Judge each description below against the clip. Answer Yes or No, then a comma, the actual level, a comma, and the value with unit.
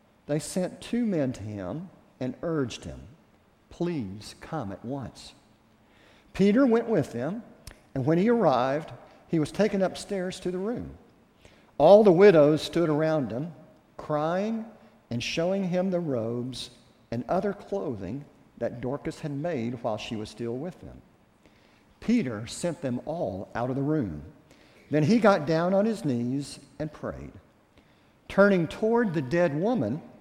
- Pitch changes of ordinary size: No, wide, 7.7 semitones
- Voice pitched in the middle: Yes, medium, 155 Hz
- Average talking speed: Yes, average, 150 wpm